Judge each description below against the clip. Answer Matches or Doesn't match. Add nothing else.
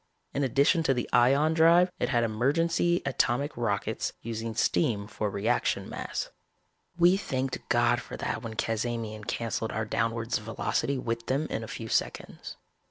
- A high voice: Doesn't match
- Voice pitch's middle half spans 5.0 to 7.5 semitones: Doesn't match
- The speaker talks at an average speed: Matches